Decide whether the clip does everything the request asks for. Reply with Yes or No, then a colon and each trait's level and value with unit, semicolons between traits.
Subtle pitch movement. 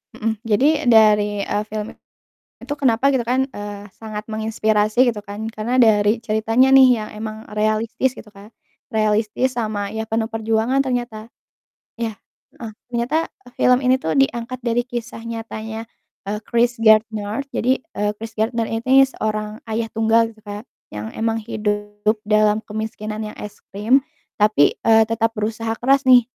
Yes: narrow, 1.8 semitones